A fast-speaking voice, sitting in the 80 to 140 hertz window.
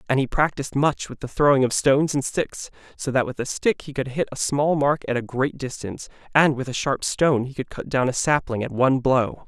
Yes: fast, 255 wpm; low, 135 Hz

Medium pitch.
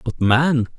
No: low, 130 Hz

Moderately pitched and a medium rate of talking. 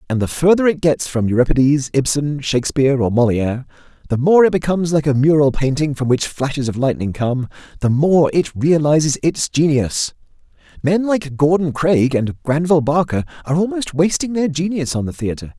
Yes: medium, 145 Hz; average, 170 wpm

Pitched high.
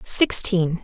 No: medium, 180 Hz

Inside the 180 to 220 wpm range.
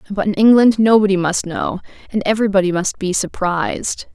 No: average, 160 wpm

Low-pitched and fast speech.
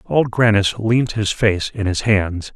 No: low, 105 Hz; average, 190 wpm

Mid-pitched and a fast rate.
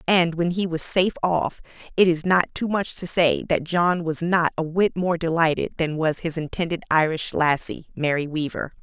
No: medium, 165 Hz; average, 195 wpm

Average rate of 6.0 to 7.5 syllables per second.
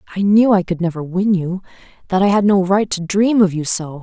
No: 5.6 syllables/s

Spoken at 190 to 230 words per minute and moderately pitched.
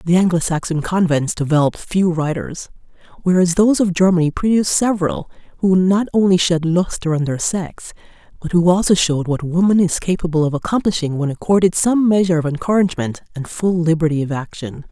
No: average, 170 wpm; medium, 170 Hz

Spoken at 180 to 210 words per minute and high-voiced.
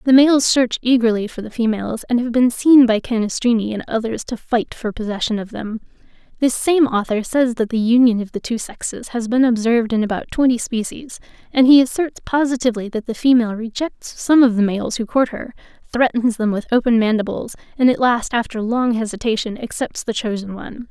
Yes: average, 200 wpm; high, 235 Hz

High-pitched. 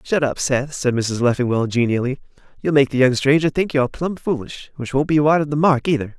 No: low, 135 Hz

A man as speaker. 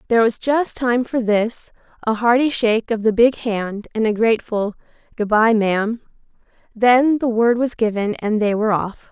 No: female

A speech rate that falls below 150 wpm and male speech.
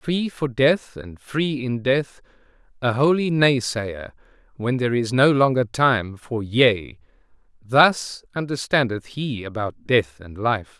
Yes: average, 140 wpm; male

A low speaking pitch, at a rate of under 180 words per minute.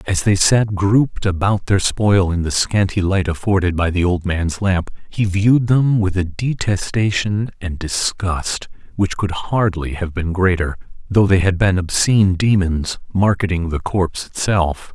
Yes: very low, 95 Hz; average, 165 wpm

